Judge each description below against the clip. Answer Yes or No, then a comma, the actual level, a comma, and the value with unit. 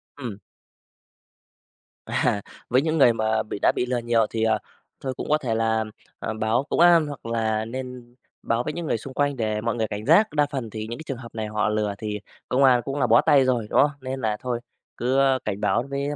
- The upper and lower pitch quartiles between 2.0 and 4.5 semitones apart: Yes, average, 3.6 semitones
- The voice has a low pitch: Yes, low, 120 Hz